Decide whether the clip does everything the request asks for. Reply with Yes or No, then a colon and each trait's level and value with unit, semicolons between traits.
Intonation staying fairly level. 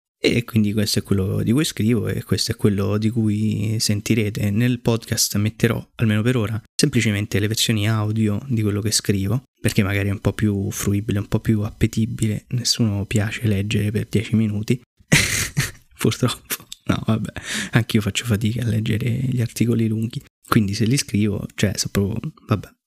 Yes: narrow, 1.9 semitones